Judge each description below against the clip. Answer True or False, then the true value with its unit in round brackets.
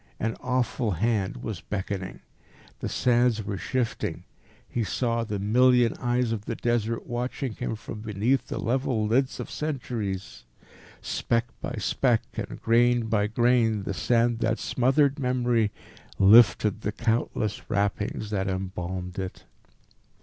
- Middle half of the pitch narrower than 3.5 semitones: True (3.0 semitones)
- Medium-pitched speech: False (115 Hz)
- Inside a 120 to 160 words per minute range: True (135 wpm)